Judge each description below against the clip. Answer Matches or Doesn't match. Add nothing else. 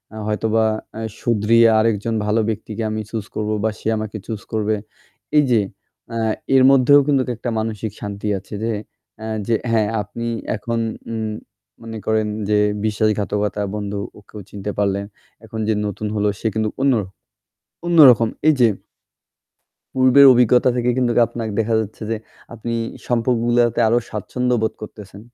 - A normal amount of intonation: Doesn't match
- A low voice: Matches